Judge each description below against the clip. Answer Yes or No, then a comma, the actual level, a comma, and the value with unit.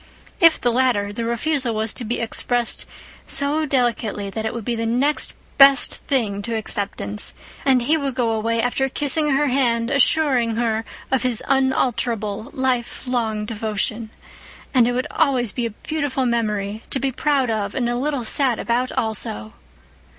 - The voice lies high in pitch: Yes, high, 240 Hz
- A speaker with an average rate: Yes, average, 165 wpm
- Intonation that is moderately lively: Yes, average, 3.4 semitones